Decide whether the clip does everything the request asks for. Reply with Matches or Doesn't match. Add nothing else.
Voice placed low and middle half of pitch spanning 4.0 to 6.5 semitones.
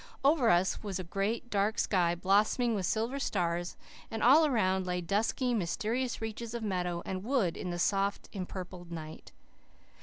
Doesn't match